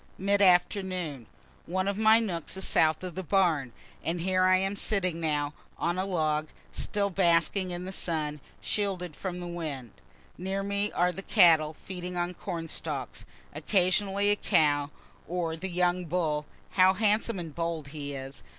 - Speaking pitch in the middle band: Yes, medium, 180 Hz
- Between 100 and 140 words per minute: No, average, 165 wpm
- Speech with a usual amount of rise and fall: Yes, average, 3.1 semitones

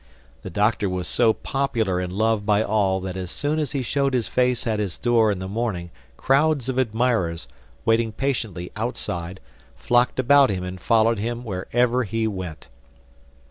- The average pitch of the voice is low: Yes, low, 110 Hz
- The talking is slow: No, average, 170 wpm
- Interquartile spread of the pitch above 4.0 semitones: Yes, average, 4.7 semitones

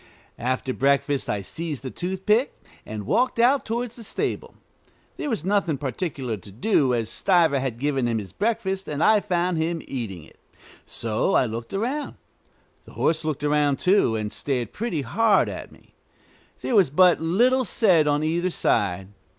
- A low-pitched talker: No, medium, 155 Hz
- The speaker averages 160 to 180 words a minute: Yes, average, 165 wpm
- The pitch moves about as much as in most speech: No, wide, 7.6 semitones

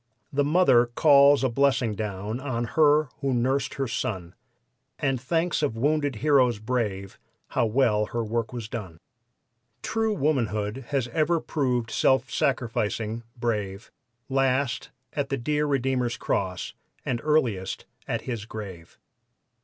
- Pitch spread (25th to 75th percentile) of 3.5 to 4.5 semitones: Yes, average, 4.2 semitones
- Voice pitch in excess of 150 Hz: No, low, 125 Hz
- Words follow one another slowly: Yes, slow, 130 wpm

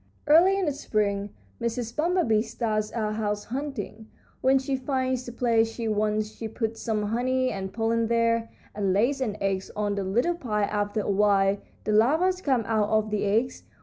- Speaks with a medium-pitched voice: No, high, 225 Hz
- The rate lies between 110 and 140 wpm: No, average, 180 wpm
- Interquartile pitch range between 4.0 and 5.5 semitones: No, average, 3.6 semitones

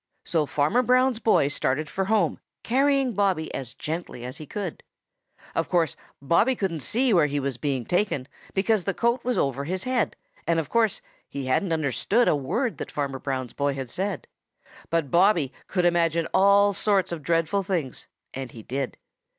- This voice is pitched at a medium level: Yes, medium, 170 Hz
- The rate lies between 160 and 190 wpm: Yes, average, 175 wpm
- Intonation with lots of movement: Yes, wide, 6.5 semitones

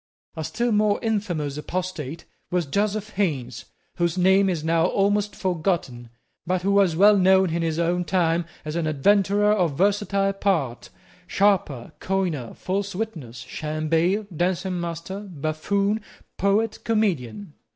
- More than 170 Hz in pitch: Yes, medium, 185 Hz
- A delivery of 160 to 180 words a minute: No, slow, 135 wpm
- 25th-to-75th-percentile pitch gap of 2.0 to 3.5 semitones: No, average, 3.9 semitones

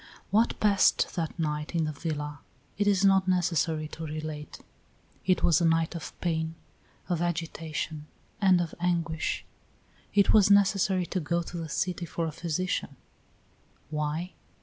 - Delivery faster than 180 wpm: No, average, 150 wpm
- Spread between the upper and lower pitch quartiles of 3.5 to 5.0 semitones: No, average, 2.7 semitones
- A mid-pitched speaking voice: Yes, medium, 170 Hz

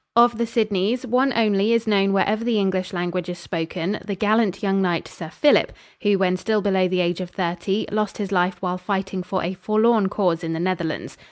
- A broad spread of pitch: No, average, 2.9 semitones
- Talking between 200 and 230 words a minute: Yes, fast, 205 wpm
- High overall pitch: Yes, high, 195 Hz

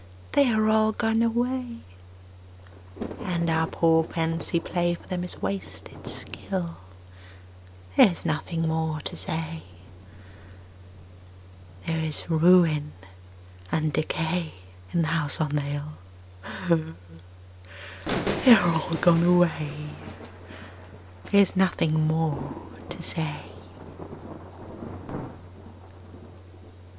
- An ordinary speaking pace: No, slow, 95 wpm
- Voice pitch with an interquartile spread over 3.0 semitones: No, average, 2.7 semitones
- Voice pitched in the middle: Yes, medium, 165 Hz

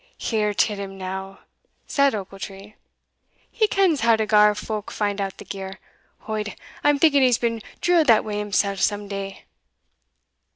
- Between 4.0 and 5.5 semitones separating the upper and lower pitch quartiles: No, average, 2.8 semitones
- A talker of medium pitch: No, high, 210 Hz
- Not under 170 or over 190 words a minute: No, average, 155 wpm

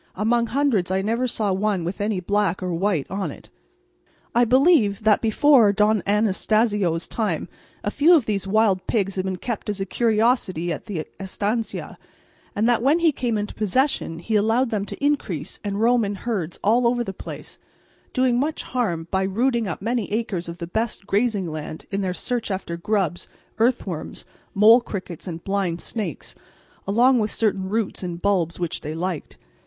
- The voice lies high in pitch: Yes, high, 205 Hz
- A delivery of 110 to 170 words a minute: No, average, 180 wpm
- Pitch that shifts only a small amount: No, average, 3.9 semitones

